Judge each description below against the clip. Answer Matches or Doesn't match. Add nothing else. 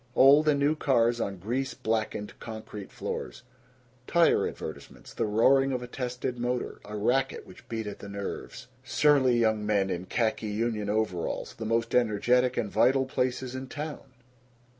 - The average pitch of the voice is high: Doesn't match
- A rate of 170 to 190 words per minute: Doesn't match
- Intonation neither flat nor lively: Matches